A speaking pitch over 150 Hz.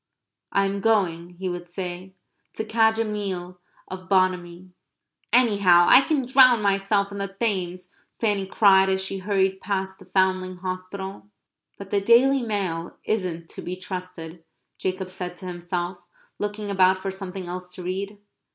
Yes: high, 190 Hz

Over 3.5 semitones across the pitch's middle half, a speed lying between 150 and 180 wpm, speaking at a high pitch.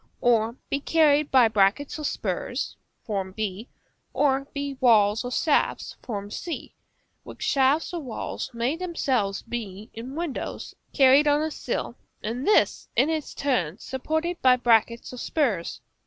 No: average, 4.5 semitones; average, 140 wpm; very high, 260 Hz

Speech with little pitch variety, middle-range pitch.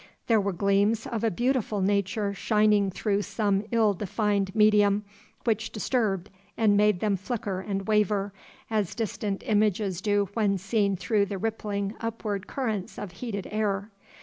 No: narrow, 1.6 semitones; high, 205 Hz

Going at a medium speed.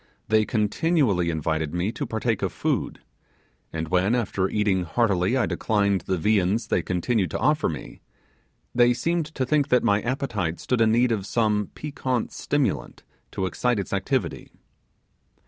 Yes: average, 155 wpm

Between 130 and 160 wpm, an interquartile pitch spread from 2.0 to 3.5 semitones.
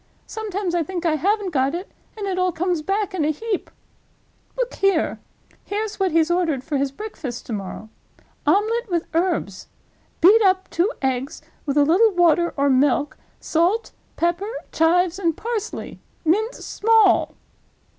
No: average, 155 wpm; average, 4.6 semitones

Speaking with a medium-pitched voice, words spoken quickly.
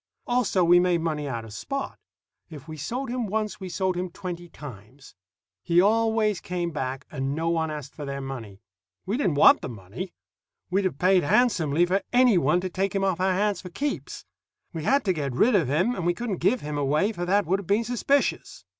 Yes: medium, 175 Hz; fast, 215 wpm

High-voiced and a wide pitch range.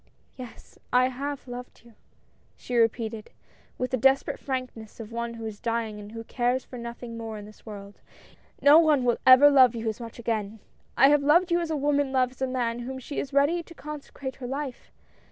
No: very high, 250 Hz; average, 3.3 semitones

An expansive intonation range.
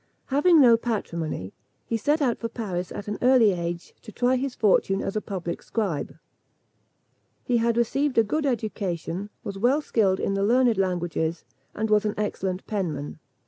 No: average, 4.5 semitones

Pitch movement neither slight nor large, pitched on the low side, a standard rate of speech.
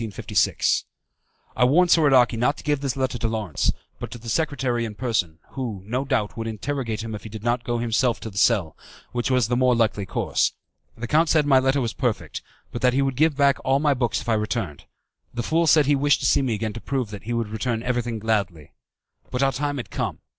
No: average, 3.5 semitones; low, 120 Hz; fast, 235 wpm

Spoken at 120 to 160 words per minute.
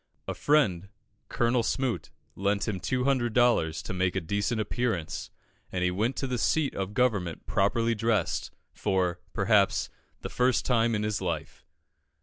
Yes: average, 150 wpm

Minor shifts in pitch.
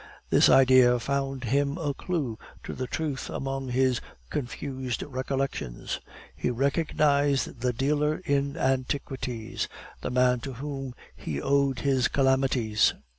Yes: narrow, 1.9 semitones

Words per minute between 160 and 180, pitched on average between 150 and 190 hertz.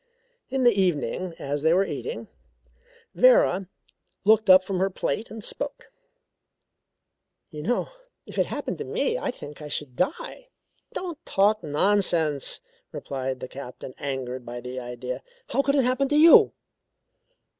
No: average, 145 wpm; medium, 185 Hz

